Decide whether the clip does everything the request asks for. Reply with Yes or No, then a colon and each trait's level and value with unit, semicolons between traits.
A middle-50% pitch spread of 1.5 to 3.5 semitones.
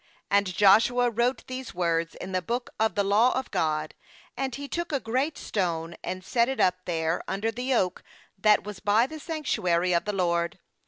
No: wide, 5.6 semitones